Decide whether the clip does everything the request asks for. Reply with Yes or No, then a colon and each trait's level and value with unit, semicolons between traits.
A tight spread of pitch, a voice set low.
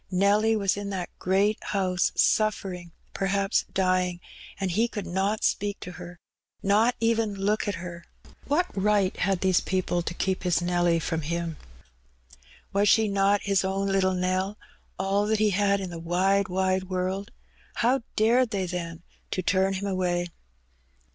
No: narrow, 2.0 semitones; high, 195 Hz